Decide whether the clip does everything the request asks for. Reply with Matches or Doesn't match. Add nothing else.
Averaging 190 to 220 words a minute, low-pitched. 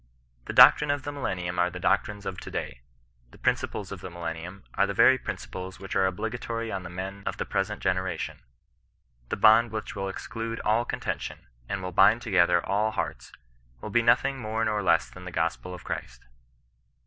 Matches